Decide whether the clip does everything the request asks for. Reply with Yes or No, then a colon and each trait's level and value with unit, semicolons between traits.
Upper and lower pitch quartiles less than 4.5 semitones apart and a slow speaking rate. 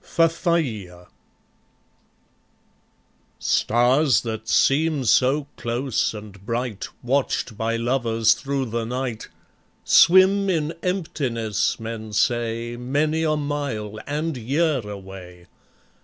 No: average, 4.9 semitones; slow, 95 wpm